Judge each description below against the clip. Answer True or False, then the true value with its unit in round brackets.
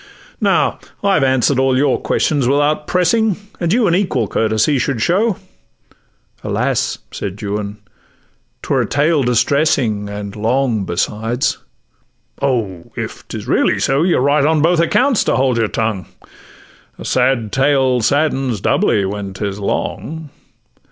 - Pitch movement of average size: False (5.9 semitones)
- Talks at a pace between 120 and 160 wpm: True (135 wpm)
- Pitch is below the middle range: True (130 Hz)